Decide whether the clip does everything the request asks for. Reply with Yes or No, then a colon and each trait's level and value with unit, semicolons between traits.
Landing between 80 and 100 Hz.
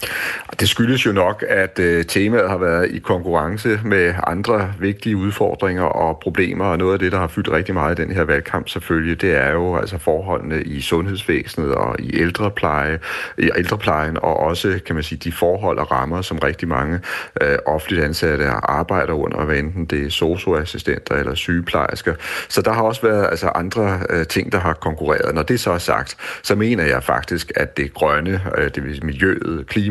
Yes: very low, 85 Hz